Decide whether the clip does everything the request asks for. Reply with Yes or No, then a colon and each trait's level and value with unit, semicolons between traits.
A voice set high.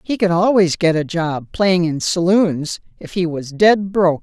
No: medium, 175 Hz